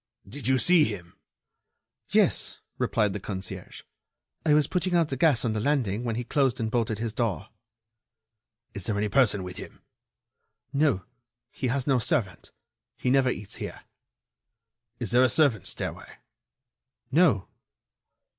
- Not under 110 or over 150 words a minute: Yes, average, 145 wpm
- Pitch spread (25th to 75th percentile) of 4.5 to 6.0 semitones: Yes, average, 4.9 semitones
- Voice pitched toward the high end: No, low, 120 Hz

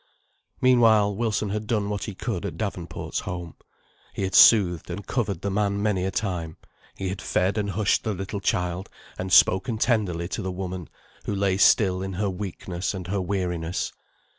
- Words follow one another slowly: No, average, 180 wpm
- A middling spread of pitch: No, narrow, 2.3 semitones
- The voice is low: Yes, very low, 95 Hz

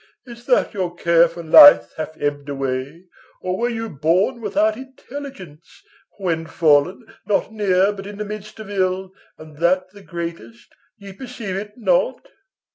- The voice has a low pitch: No, high, 190 Hz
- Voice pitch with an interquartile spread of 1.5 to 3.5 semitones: No, average, 4.5 semitones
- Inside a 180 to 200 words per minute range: No, average, 155 wpm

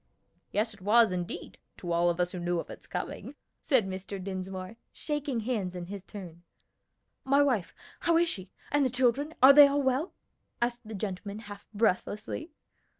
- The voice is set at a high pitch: Yes, high, 210 Hz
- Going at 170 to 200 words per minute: Yes, average, 175 wpm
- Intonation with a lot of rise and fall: Yes, wide, 6.0 semitones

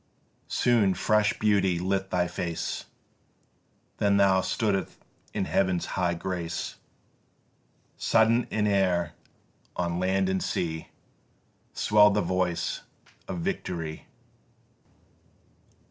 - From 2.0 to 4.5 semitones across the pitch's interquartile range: Yes, average, 2.9 semitones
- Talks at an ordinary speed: No, slow, 95 wpm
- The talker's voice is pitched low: Yes, very low, 95 Hz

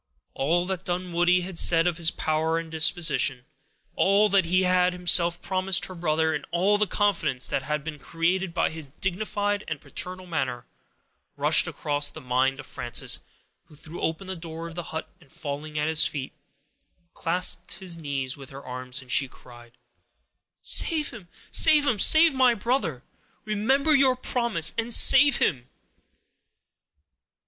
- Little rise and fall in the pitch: No, average, 4.4 semitones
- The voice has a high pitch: No, medium, 170 Hz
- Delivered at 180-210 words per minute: No, average, 155 wpm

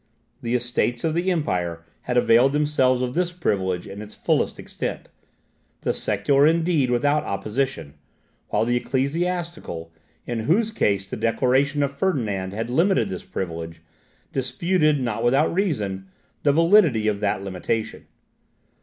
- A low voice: Yes, low, 125 Hz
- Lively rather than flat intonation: Yes, wide, 6.9 semitones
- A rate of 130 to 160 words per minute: Yes, slow, 135 wpm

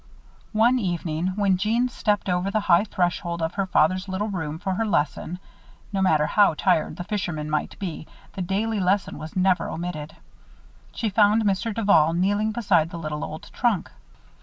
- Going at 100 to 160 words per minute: No, average, 170 wpm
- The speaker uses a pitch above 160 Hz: Yes, medium, 185 Hz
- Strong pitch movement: No, average, 3.6 semitones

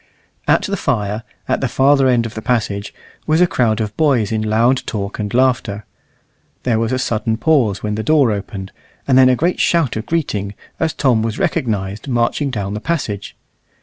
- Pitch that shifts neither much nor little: Yes, average, 4.0 semitones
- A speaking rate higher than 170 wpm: Yes, average, 190 wpm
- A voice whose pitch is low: Yes, low, 115 Hz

